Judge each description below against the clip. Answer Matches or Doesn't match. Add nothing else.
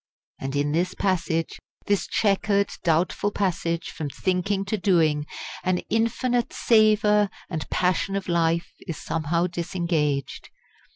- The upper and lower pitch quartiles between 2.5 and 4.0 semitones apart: Matches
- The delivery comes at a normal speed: Doesn't match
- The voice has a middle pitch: Matches